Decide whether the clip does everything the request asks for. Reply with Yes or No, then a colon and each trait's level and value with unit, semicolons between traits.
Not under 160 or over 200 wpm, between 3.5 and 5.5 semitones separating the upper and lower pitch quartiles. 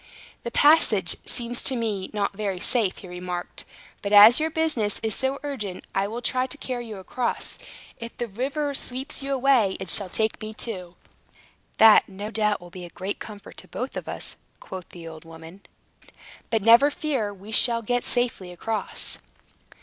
Yes: average, 180 wpm; average, 4.4 semitones